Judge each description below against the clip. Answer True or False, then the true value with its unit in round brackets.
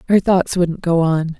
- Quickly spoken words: True (215 wpm)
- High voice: False (175 Hz)